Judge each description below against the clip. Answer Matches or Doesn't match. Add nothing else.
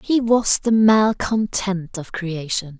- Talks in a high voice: Matches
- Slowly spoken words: Matches